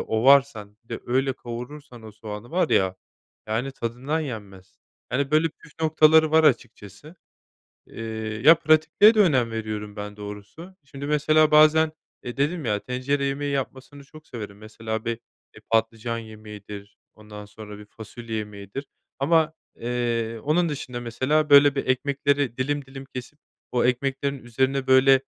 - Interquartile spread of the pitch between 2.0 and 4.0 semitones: No, average, 4.7 semitones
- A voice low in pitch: Yes, low, 130 Hz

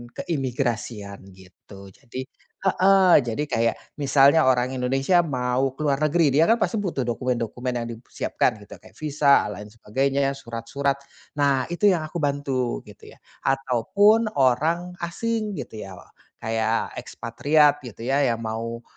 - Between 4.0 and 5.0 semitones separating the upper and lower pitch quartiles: Yes, average, 4.5 semitones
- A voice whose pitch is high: No, low, 135 Hz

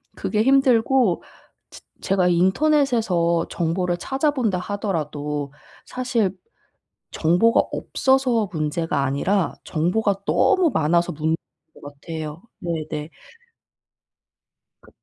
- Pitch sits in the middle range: Yes, medium, 180 Hz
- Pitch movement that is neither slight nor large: No, wide, 6.2 semitones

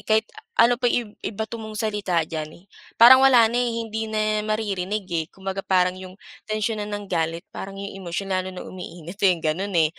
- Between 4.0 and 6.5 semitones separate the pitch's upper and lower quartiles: No, average, 3.2 semitones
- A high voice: Yes, high, 200 Hz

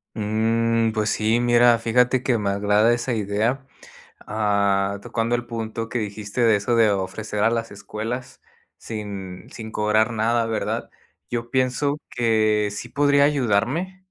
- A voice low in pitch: Yes, low, 115 Hz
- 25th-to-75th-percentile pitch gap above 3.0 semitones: No, narrow, 2.4 semitones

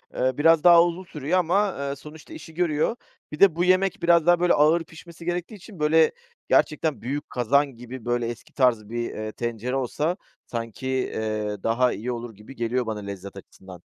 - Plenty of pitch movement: Yes, wide, 6.2 semitones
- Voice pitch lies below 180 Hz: Yes, medium, 140 Hz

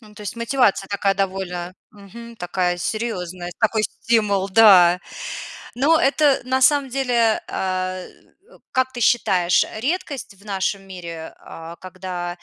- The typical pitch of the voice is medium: No, high, 200 Hz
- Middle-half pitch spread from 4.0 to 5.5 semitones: Yes, average, 4.4 semitones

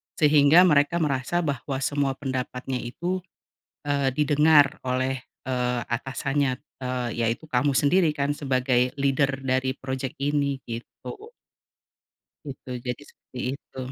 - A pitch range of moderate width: No, narrow, 2.2 semitones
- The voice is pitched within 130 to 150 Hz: Yes, low, 135 Hz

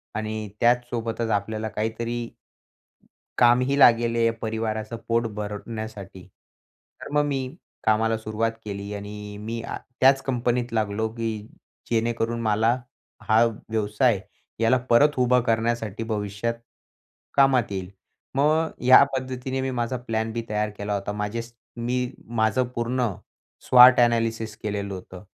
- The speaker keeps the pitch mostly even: Yes, narrow, 2.1 semitones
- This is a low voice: Yes, low, 115 Hz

